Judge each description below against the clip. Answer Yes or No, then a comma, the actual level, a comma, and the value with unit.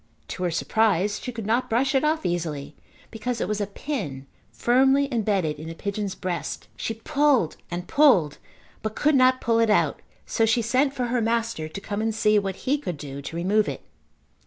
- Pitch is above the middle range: Yes, high, 220 Hz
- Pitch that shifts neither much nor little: No, wide, 5.7 semitones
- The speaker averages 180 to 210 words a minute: Yes, average, 200 wpm